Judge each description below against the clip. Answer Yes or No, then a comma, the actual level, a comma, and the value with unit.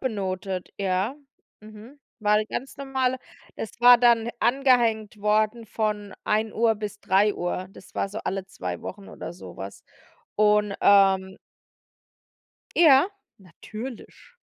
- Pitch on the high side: Yes, high, 215 Hz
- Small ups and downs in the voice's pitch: No, average, 3.3 semitones